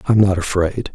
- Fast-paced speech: No, average, 190 wpm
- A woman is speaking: No, male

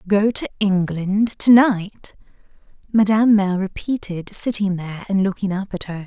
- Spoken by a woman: Yes, female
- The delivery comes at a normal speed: Yes, average, 150 wpm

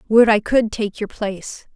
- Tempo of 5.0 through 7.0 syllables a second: No, 4.7 syllables/s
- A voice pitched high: Yes, high, 215 Hz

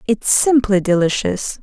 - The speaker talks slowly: Yes, slow, 110 wpm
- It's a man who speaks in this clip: No, female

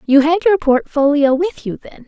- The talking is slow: No, average, 200 wpm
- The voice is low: No, very high, 300 Hz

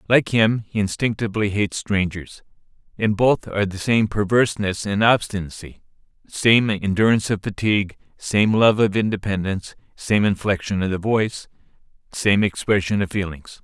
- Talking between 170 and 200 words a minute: No, slow, 135 wpm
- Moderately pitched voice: No, low, 100 Hz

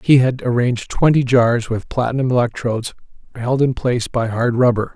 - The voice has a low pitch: Yes, low, 125 Hz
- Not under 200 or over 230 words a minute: No, average, 170 wpm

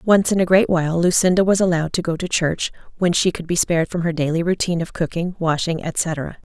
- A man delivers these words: No, female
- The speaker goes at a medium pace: No, fast, 230 wpm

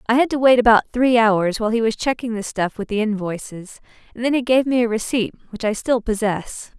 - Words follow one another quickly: Yes, fast, 240 wpm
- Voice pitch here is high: Yes, high, 225 Hz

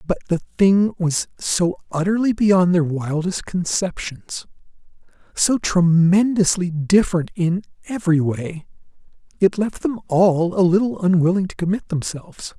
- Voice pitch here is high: No, medium, 180 Hz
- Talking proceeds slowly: Yes, slow, 125 wpm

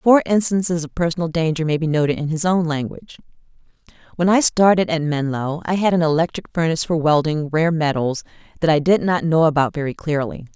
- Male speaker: No, female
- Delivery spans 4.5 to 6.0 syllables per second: Yes, 5.9 syllables/s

